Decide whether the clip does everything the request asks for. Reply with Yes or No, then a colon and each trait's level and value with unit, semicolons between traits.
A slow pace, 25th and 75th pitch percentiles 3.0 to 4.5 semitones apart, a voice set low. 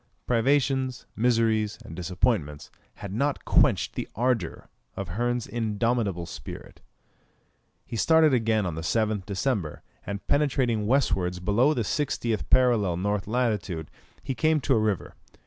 Yes: slow, 130 wpm; average, 4.1 semitones; low, 115 Hz